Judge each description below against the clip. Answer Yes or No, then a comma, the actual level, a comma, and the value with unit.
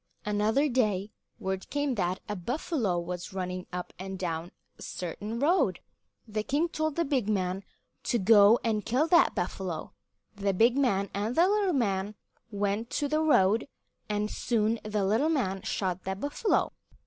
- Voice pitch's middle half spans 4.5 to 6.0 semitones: Yes, wide, 5.5 semitones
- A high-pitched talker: Yes, high, 210 Hz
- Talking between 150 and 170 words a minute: Yes, average, 160 wpm